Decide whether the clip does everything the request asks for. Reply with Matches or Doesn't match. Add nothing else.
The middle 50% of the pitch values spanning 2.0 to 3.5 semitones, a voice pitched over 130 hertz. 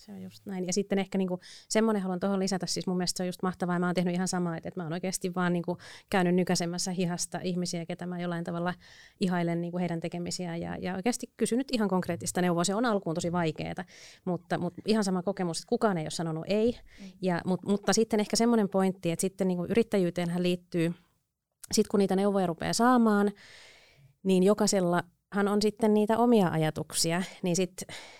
Matches